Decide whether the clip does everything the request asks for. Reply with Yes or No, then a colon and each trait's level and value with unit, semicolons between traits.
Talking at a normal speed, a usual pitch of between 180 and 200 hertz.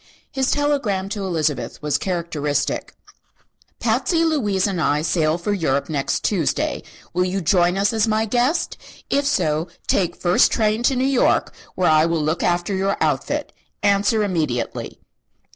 Yes: average, 150 wpm; high, 190 Hz